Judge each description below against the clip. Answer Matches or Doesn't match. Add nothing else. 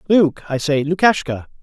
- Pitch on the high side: Doesn't match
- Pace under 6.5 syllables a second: Matches